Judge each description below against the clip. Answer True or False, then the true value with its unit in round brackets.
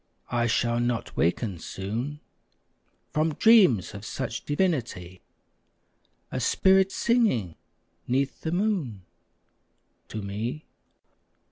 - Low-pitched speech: True (125 Hz)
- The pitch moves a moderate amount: False (7.9 semitones)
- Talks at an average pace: False (95 wpm)